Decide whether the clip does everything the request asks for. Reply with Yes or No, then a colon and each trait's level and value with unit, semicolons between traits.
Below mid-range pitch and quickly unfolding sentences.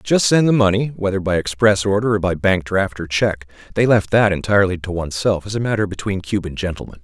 Yes: low, 100 Hz; fast, 220 wpm